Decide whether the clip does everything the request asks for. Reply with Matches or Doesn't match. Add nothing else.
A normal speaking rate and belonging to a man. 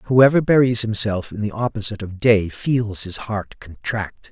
Matches